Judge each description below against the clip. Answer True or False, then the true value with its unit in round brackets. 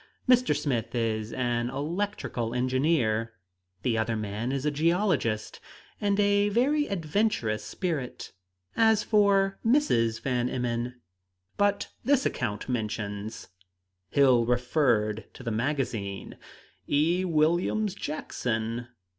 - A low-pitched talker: True (130 Hz)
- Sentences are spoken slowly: True (110 wpm)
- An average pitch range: False (8.7 semitones)